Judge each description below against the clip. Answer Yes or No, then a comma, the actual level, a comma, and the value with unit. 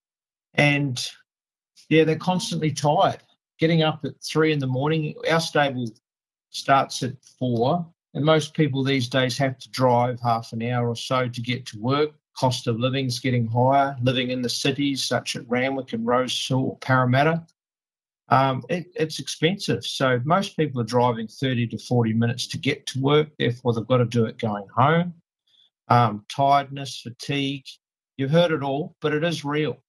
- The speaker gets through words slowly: No, average, 175 wpm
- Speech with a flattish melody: No, average, 3.8 semitones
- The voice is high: No, low, 135 Hz